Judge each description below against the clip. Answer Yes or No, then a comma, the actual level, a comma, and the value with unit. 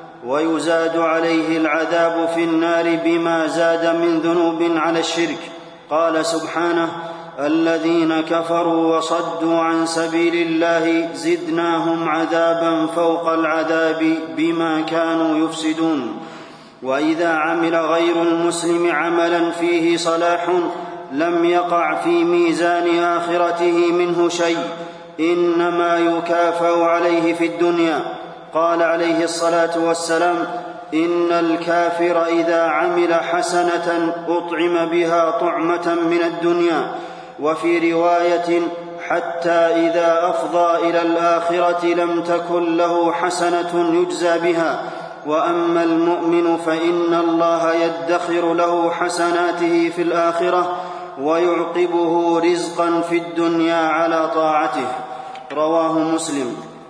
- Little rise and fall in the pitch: Yes, narrow, 0.6 semitones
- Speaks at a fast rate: No, average, 95 wpm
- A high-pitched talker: No, medium, 170 Hz